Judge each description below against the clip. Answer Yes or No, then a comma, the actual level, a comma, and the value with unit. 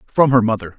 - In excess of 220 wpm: Yes, fast, 230 wpm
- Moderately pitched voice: No, low, 120 Hz